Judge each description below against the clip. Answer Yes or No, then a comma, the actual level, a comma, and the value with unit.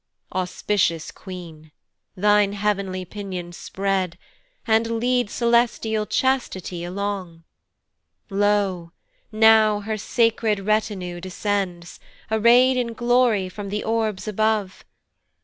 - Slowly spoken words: Yes, slow, 95 wpm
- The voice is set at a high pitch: Yes, high, 205 Hz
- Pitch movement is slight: No, average, 3.0 semitones